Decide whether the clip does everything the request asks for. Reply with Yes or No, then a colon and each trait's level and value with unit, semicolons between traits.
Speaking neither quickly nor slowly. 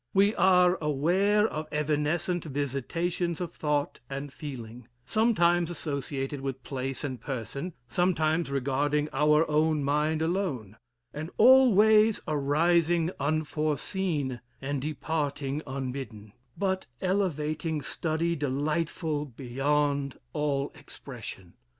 No: slow, 100 wpm